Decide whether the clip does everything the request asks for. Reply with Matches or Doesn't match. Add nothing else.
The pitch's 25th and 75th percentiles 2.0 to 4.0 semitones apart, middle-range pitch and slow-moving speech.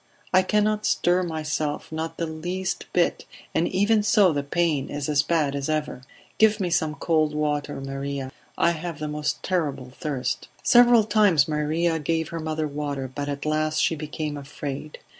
Doesn't match